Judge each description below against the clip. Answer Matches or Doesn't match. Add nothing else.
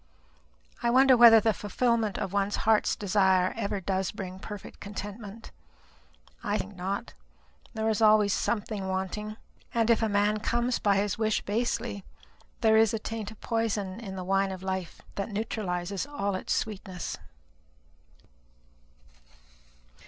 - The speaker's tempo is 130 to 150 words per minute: Matches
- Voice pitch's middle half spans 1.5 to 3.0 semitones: Matches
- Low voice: Doesn't match